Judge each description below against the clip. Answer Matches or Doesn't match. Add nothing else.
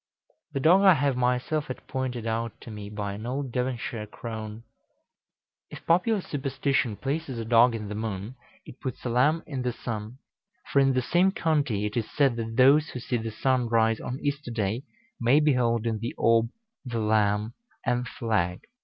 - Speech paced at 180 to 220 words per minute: Matches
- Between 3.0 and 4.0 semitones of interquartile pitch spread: Matches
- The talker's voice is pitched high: Doesn't match